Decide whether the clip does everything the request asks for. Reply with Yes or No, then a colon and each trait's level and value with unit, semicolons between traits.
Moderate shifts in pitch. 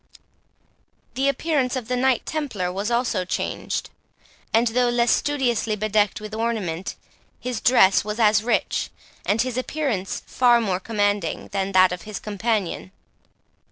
Yes: average, 3.7 semitones